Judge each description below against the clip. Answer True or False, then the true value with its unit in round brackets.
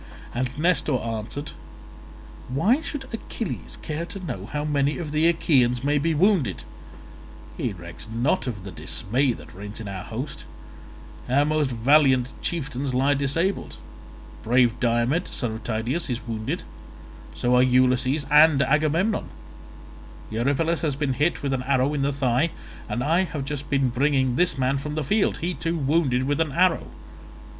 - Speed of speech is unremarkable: True (155 wpm)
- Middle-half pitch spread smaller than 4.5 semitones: True (3.9 semitones)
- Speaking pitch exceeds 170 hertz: False (140 Hz)